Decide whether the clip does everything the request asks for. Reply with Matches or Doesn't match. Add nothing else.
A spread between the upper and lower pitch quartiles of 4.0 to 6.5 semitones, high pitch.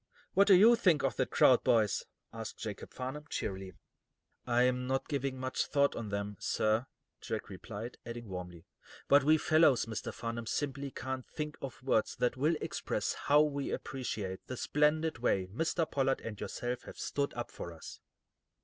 Doesn't match